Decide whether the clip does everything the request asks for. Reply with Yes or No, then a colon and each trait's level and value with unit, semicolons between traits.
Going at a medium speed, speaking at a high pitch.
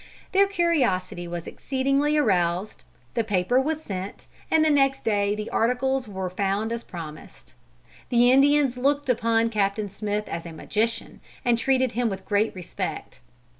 Yes: average, 150 wpm; high, 230 Hz